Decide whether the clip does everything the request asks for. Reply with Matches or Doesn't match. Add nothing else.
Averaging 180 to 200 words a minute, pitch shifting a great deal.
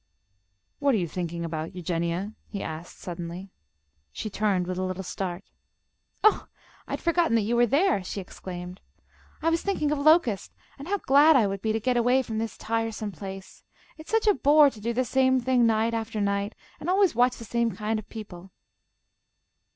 Matches